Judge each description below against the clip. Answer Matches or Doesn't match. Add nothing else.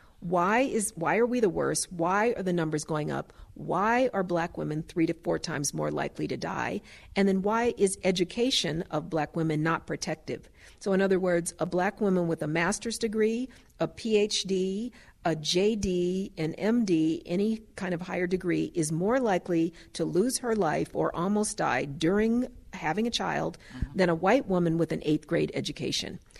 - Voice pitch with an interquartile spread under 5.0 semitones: Matches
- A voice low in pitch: Doesn't match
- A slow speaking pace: Doesn't match